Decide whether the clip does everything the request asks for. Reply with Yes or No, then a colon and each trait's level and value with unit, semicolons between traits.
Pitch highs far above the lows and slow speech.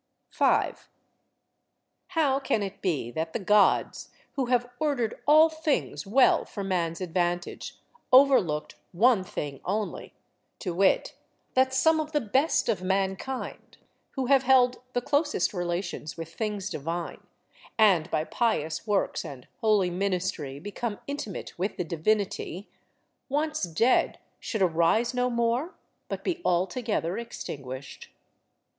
Yes: wide, 6.6 semitones; slow, 125 wpm